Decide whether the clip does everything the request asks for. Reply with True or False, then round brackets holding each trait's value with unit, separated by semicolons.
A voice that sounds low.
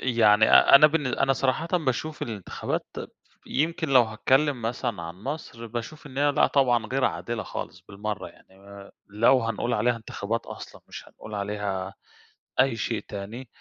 True (115 Hz)